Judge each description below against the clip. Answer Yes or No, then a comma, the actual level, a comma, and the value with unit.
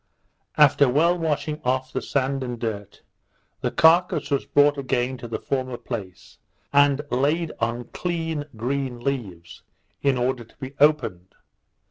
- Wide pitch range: No, average, 3.3 semitones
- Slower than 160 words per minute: Yes, average, 140 wpm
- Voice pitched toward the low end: Yes, low, 130 Hz